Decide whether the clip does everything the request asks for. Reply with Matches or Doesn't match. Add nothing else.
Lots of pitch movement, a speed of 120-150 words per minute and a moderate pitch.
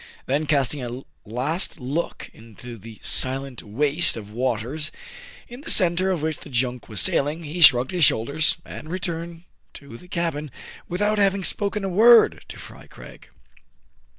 Doesn't match